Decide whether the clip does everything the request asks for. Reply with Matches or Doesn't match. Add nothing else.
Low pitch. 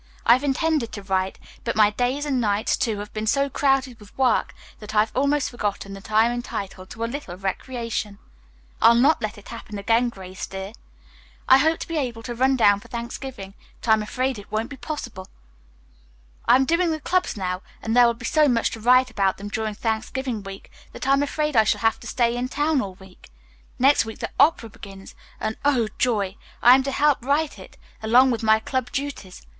Doesn't match